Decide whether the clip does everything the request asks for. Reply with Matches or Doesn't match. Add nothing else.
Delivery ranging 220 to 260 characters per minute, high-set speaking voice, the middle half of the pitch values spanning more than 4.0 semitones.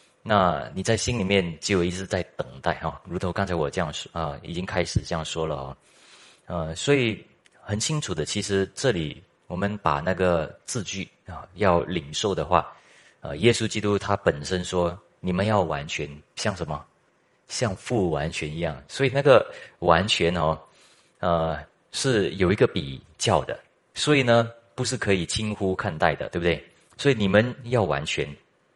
Doesn't match